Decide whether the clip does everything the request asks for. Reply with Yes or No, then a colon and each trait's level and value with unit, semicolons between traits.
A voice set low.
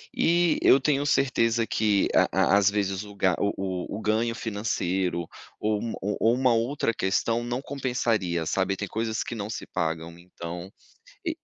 Yes: low, 110 Hz